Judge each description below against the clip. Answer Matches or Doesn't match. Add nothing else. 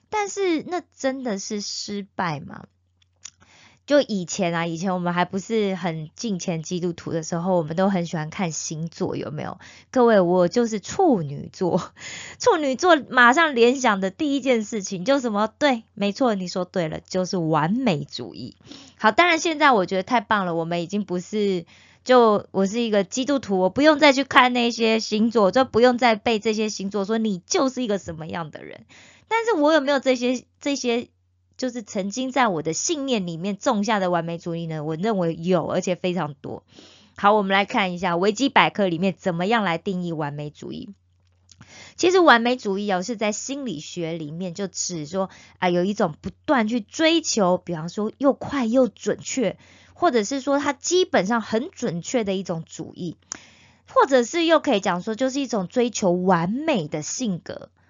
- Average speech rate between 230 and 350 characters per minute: Matches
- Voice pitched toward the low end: Doesn't match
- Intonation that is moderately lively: Doesn't match